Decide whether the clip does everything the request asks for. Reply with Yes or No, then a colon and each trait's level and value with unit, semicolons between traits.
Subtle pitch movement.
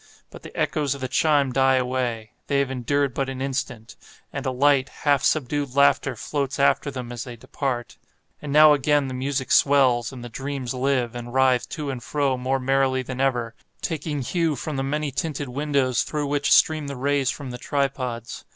Yes: narrow, 2.0 semitones